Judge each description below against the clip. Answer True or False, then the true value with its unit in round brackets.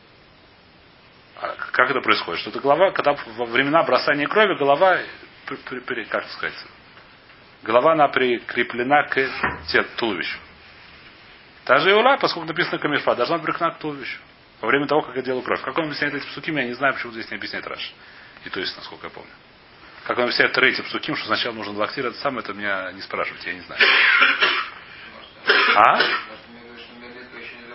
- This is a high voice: False (135 Hz)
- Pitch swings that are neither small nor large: True (3.7 semitones)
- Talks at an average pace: False (165 wpm)